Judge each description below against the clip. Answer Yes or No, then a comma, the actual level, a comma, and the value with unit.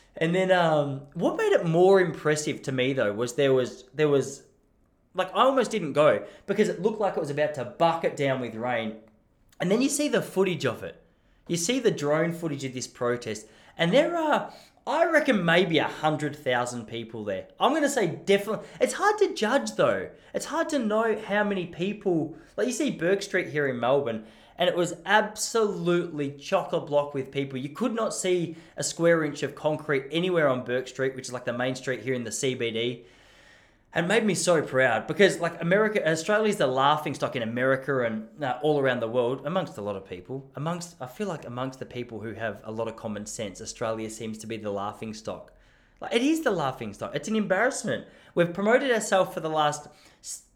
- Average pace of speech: No, fast, 210 wpm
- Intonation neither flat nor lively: No, wide, 7.3 semitones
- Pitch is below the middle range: No, medium, 150 Hz